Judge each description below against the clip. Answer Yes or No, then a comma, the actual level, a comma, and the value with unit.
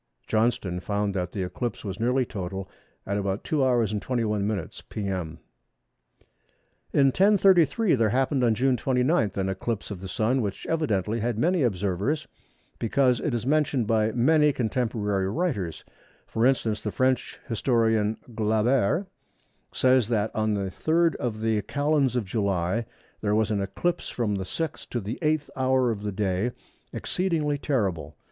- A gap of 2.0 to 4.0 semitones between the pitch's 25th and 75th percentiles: No, average, 4.5 semitones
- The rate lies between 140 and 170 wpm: Yes, average, 150 wpm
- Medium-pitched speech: No, low, 115 Hz